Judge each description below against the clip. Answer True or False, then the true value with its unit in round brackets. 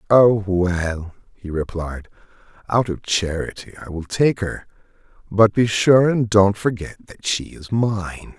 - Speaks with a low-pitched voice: True (100 Hz)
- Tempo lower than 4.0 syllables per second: True (3.8 syllables/s)